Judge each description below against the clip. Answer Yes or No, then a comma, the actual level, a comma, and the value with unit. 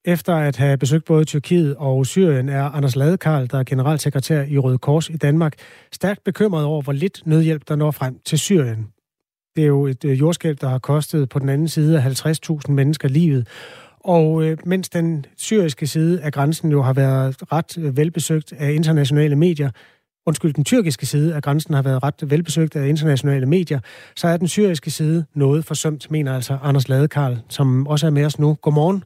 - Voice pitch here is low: No, medium, 150 Hz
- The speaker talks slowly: No, average, 190 wpm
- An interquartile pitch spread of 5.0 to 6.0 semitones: No, narrow, 2.4 semitones